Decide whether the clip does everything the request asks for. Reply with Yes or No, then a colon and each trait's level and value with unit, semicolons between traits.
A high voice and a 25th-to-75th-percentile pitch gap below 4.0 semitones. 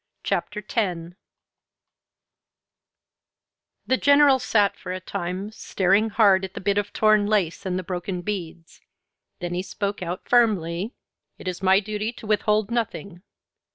Yes: high, 200 Hz; average, 2.9 semitones